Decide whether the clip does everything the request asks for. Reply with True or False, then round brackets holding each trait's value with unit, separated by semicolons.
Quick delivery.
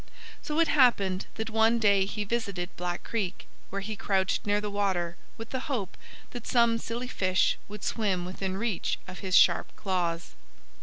False (170 wpm)